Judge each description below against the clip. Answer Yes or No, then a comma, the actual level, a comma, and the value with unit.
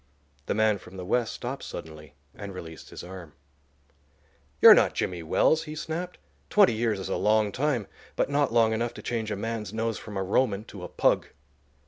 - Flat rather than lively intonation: No, average, 4.0 semitones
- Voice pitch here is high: No, low, 110 Hz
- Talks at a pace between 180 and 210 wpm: Yes, average, 190 wpm